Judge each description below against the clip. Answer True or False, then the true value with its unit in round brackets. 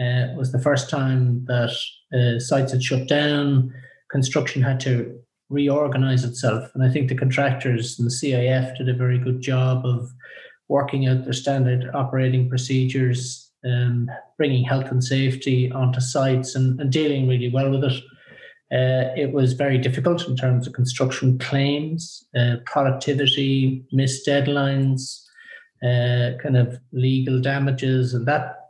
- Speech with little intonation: True (1.5 semitones)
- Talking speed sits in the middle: True (150 wpm)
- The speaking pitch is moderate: False (130 Hz)